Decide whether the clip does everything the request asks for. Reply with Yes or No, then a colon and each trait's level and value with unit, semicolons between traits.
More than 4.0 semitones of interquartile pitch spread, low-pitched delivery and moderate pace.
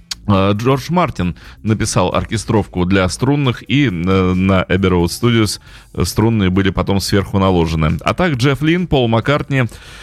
Yes: average, 5.2 semitones; low, 100 Hz; average, 125 wpm